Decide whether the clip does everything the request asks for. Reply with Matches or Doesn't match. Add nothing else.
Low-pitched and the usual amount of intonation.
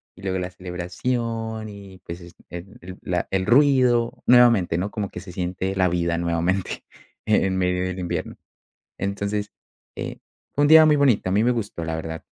Matches